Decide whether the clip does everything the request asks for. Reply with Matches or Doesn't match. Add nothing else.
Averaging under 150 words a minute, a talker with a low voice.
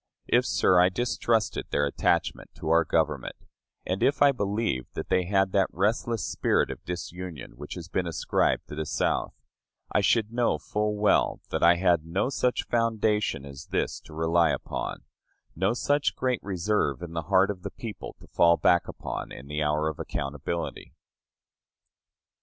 Doesn't match